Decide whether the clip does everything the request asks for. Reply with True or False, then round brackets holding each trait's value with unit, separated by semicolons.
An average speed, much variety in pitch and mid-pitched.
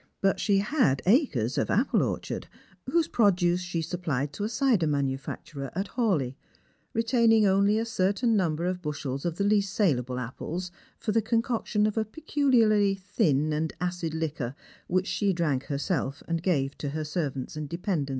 True (165 wpm; 6.0 semitones; 180 Hz)